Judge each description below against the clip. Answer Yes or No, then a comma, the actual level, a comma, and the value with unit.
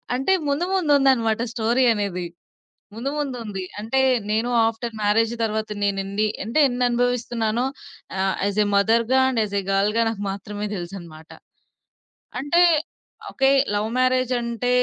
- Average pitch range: Yes, average, 3.6 semitones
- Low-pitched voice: No, high, 225 Hz